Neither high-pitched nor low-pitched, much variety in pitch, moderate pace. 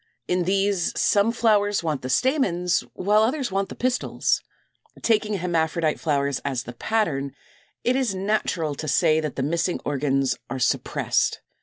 Yes: medium, 180 Hz; wide, 6.3 semitones; average, 150 wpm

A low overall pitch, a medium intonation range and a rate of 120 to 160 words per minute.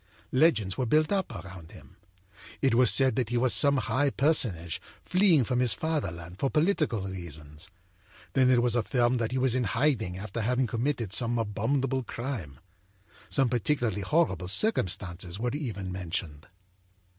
No: low, 120 Hz; wide, 6.0 semitones; average, 155 wpm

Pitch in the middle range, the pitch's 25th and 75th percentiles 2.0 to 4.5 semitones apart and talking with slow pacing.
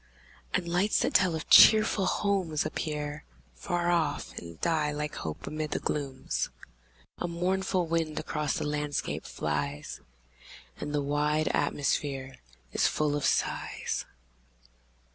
Yes: medium, 150 Hz; average, 2.9 semitones; slow, 125 wpm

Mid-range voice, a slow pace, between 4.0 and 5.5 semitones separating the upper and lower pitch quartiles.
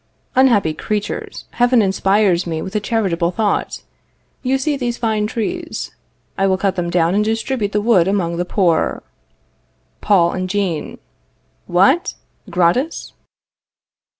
No: high, 200 Hz; slow, 130 wpm; average, 4.4 semitones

